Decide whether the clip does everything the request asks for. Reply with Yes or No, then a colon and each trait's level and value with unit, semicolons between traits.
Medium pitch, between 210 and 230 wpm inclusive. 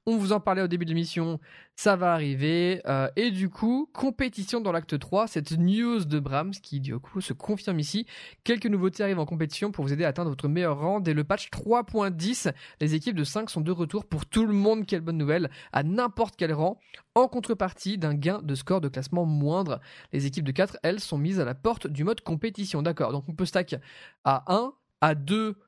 Yes: medium, 180 Hz; fast, 220 wpm